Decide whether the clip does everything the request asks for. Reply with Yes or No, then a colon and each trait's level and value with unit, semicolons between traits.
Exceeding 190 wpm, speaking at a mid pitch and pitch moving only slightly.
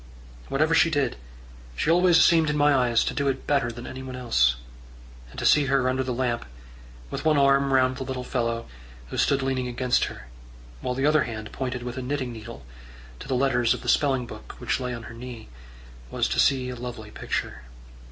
No: fast, 205 wpm; low, 130 Hz; narrow, 2.2 semitones